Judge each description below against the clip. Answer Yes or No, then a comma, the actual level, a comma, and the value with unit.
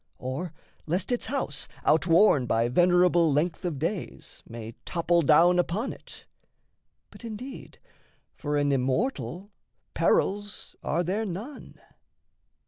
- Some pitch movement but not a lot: No, wide, 5.7 semitones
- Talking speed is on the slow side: Yes, slow, 115 wpm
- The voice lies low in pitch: No, medium, 175 Hz